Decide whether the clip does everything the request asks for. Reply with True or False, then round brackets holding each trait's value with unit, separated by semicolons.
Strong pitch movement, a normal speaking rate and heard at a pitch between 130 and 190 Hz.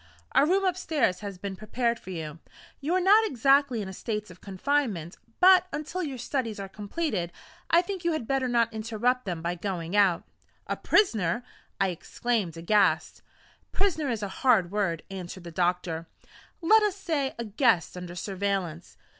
False (7.7 semitones; 170 wpm; 215 Hz)